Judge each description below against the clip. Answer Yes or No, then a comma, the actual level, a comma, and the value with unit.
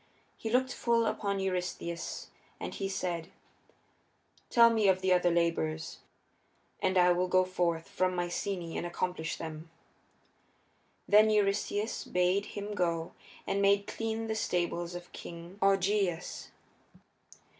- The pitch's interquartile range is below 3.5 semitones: Yes, average, 2.8 semitones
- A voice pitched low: No, medium, 185 Hz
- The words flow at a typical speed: No, slow, 125 wpm